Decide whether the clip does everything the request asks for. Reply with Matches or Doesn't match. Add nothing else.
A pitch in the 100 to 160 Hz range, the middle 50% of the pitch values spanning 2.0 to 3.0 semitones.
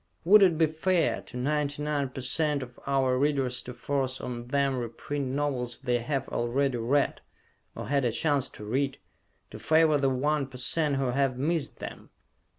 Matches